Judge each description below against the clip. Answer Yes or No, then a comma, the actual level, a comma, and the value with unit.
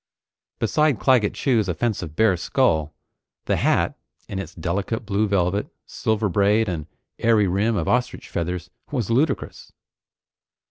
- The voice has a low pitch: Yes, low, 105 Hz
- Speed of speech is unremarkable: No, slow, 130 wpm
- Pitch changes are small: No, average, 4.2 semitones